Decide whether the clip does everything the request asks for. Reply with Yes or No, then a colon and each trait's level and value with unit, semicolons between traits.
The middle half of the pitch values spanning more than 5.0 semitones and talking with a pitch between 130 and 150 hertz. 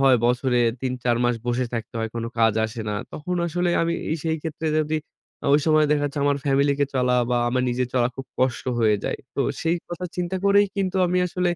Yes: wide, 5.4 semitones; medium, 140 Hz